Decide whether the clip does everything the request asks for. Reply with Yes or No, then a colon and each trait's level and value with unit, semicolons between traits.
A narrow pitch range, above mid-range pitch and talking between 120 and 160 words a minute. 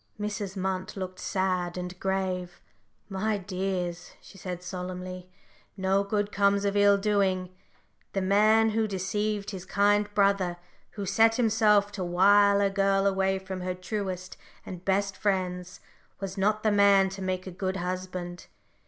Yes: narrow, 1.7 semitones; high, 195 Hz; average, 150 wpm